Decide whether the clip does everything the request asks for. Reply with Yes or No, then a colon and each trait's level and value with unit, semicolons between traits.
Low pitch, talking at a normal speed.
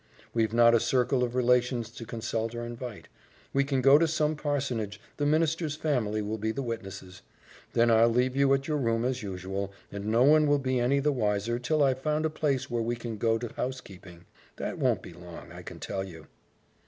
No: low, 120 Hz; fast, 210 wpm